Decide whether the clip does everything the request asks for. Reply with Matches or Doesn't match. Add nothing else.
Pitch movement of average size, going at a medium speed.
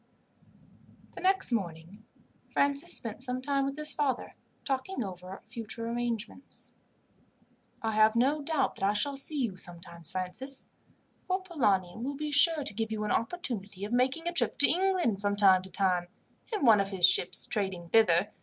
Doesn't match